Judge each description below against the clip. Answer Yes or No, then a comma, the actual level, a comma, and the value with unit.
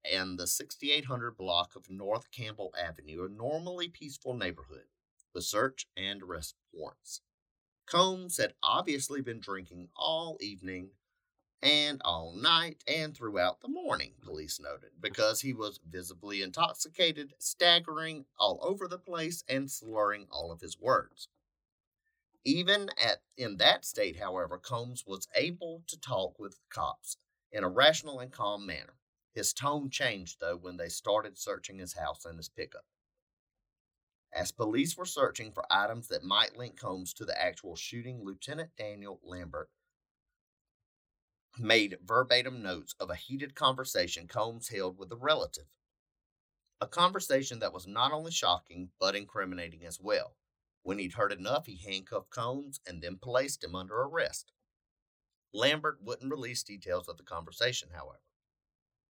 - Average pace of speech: Yes, average, 145 wpm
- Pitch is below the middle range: Yes, low, 120 Hz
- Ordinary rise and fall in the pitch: No, wide, 8.5 semitones